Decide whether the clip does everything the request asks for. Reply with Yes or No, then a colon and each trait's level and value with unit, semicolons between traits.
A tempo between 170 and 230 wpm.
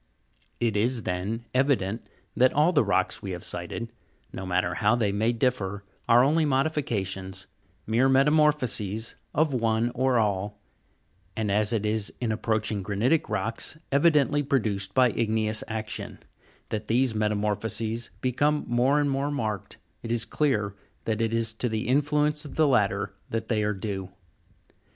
No: average, 150 wpm